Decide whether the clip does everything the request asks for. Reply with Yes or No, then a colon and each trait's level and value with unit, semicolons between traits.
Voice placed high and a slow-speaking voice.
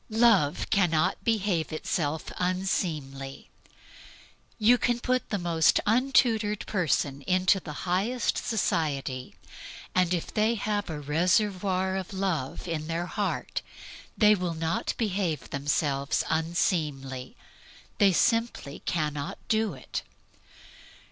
No: medium, 180 Hz; slow, 110 wpm